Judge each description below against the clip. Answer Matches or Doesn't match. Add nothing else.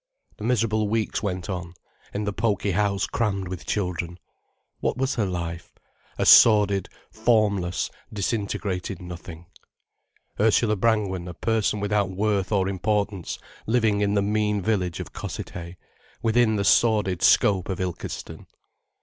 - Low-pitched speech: Matches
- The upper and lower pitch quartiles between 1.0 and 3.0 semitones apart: Matches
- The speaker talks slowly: Matches